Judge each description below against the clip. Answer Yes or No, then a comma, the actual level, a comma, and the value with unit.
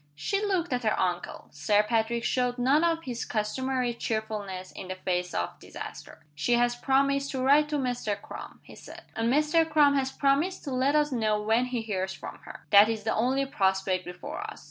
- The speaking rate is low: No, average, 200 wpm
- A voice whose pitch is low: No, high, 245 Hz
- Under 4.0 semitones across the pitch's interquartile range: No, average, 4.8 semitones